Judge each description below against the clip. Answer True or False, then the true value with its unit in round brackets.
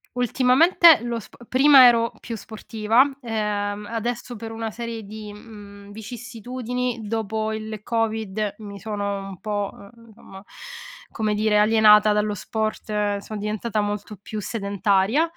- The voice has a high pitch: True (220 Hz)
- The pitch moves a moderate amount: False (2.0 semitones)